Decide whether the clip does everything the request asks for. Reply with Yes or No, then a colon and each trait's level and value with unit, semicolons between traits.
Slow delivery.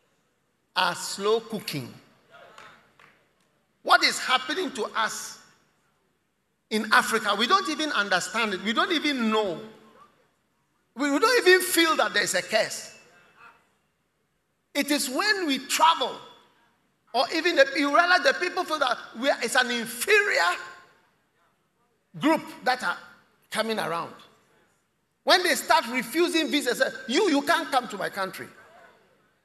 Yes: slow, 130 wpm